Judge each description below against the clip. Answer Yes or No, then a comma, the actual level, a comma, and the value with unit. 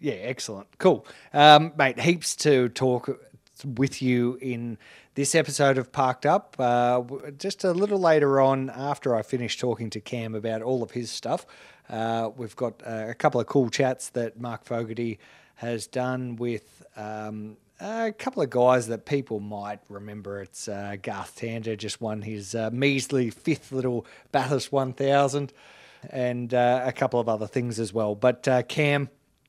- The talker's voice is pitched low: Yes, low, 125 Hz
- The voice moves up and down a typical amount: Yes, average, 3.4 semitones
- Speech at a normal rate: Yes, average, 170 wpm